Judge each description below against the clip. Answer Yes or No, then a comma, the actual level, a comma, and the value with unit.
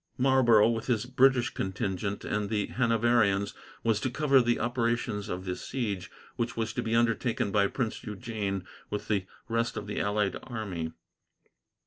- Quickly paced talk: No, average, 155 wpm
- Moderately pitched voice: No, low, 110 Hz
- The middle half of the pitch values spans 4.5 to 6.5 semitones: No, average, 2.8 semitones